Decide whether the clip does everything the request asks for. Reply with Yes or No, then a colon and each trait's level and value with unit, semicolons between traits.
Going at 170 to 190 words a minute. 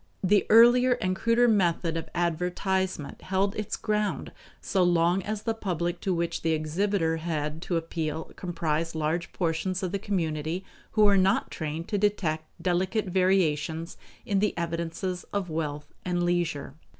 No: average, 150 wpm